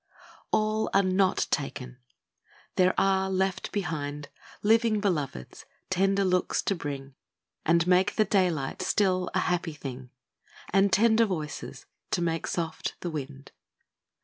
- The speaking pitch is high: No, medium, 180 Hz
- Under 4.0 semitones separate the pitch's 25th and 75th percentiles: No, average, 4.8 semitones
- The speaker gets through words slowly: Yes, slow, 130 wpm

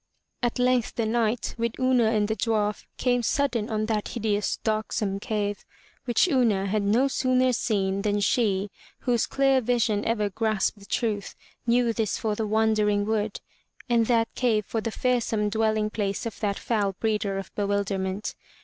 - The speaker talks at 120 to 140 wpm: No, average, 165 wpm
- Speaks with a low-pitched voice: No, high, 220 Hz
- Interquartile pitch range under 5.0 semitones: Yes, narrow, 2.4 semitones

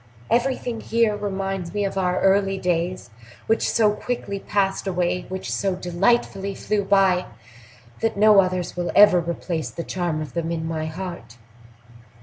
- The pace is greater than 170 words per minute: No, average, 150 wpm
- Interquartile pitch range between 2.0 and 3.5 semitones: Yes, narrow, 2.6 semitones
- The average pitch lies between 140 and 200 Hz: Yes, high, 190 Hz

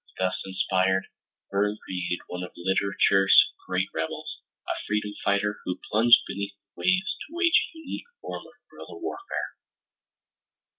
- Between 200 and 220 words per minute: No, average, 140 wpm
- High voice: No, low, 100 Hz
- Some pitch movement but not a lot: Yes, average, 4.0 semitones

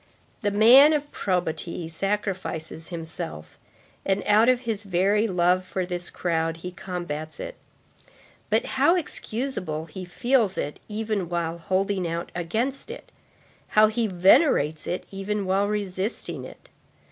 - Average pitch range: Yes, average, 3.7 semitones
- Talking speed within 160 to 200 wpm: No, slow, 135 wpm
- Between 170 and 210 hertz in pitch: Yes, high, 190 Hz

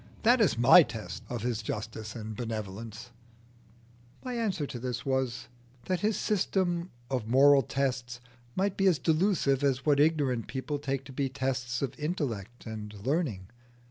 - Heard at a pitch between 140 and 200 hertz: No, low, 130 Hz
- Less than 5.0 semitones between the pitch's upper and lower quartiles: No, wide, 5.4 semitones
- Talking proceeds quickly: No, average, 145 wpm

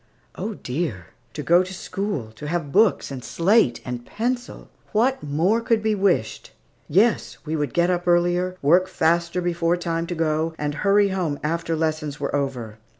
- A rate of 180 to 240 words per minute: No, average, 170 wpm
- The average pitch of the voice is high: No, medium, 170 Hz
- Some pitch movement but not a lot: Yes, average, 4.1 semitones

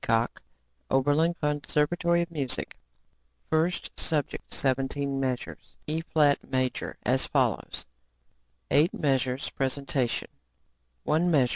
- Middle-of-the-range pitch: Yes, medium, 145 Hz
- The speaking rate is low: Yes, slow, 95 wpm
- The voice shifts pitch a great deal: No, average, 3.1 semitones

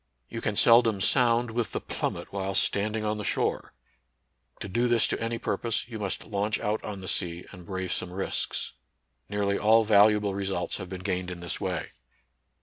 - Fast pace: No, average, 195 wpm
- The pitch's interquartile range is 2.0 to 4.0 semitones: Yes, average, 2.8 semitones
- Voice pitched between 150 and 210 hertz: No, low, 105 Hz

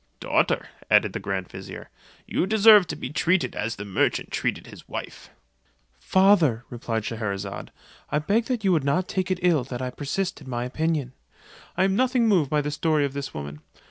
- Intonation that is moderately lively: No, wide, 7.6 semitones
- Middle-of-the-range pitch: Yes, medium, 150 Hz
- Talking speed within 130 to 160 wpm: No, average, 185 wpm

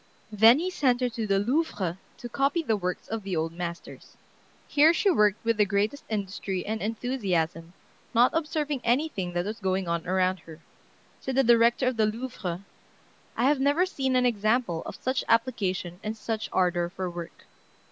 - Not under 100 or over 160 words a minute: No, average, 175 wpm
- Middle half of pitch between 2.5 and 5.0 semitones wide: No, wide, 5.6 semitones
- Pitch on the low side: No, high, 220 Hz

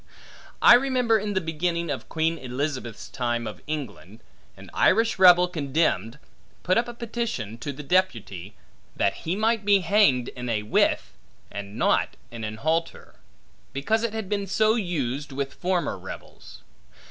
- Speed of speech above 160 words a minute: No, average, 155 wpm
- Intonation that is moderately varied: No, wide, 8.5 semitones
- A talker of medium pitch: Yes, medium, 165 Hz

